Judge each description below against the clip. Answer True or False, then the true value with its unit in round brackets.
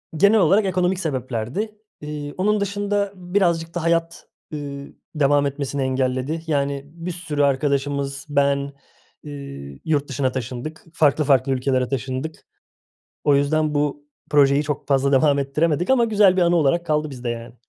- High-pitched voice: False (145 Hz)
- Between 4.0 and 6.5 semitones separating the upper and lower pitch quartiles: False (3.4 semitones)